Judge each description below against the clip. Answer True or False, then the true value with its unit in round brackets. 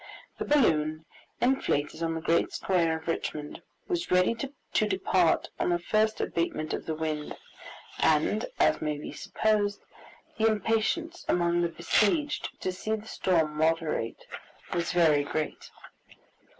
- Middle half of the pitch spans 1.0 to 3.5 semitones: False (5.3 semitones)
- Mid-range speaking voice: True (175 Hz)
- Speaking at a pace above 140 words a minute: False (135 wpm)